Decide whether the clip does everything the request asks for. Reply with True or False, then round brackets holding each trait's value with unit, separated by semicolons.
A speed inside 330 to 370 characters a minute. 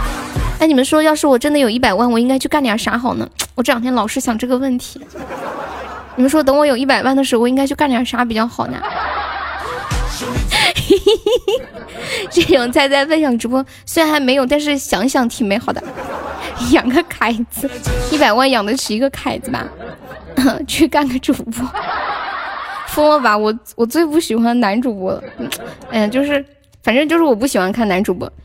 False (270 characters per minute)